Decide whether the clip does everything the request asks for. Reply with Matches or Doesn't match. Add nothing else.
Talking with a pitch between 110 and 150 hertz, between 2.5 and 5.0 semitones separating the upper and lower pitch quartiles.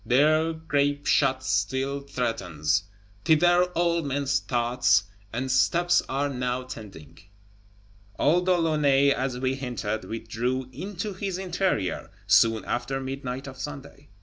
Matches